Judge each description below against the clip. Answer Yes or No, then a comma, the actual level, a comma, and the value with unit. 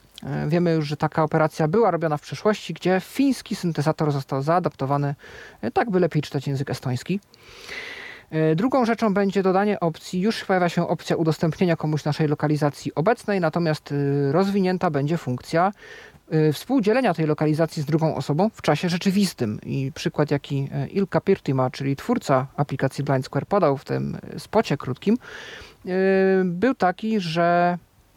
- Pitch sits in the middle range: Yes, medium, 165 Hz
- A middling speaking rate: Yes, average, 140 wpm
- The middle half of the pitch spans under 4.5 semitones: No, average, 5.0 semitones